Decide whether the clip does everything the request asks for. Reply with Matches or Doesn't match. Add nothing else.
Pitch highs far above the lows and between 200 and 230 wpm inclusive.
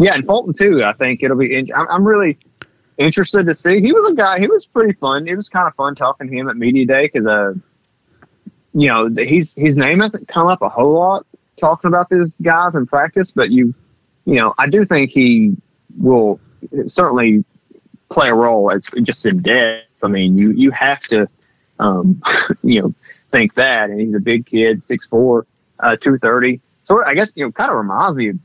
Matches